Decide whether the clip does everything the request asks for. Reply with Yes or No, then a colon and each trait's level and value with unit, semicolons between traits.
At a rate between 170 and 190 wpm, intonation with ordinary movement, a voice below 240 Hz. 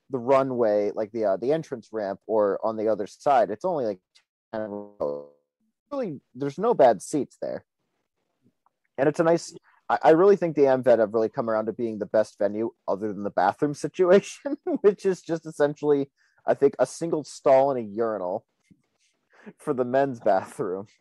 No: average, 180 wpm; wide, 7.2 semitones; low, 135 Hz